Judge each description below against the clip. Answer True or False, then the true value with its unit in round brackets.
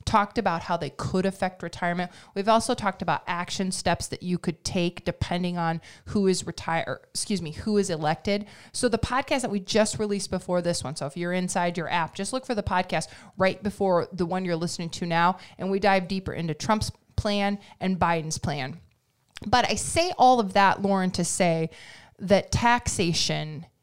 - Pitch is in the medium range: True (180 Hz)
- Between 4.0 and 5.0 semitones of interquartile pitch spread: False (2.9 semitones)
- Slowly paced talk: False (195 wpm)